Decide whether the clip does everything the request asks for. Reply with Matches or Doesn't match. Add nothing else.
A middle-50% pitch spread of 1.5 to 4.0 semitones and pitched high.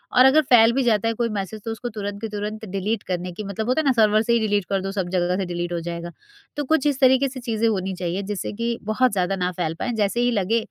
Matches